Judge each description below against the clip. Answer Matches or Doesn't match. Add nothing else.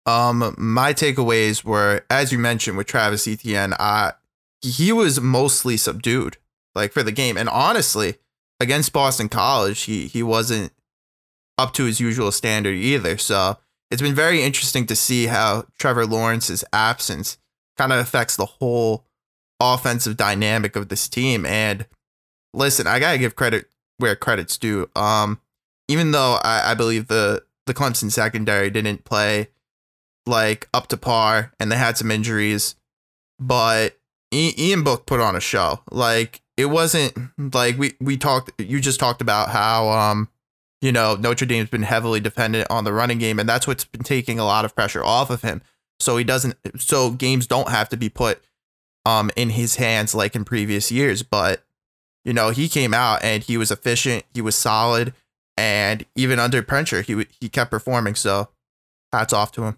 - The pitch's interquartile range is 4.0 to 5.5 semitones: Doesn't match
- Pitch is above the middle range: Doesn't match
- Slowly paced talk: Doesn't match